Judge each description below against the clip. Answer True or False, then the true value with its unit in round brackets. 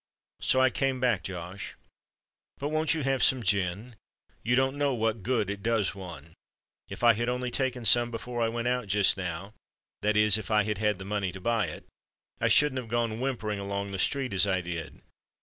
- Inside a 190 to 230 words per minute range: True (200 wpm)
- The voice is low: True (110 Hz)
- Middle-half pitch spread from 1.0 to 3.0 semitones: False (4.1 semitones)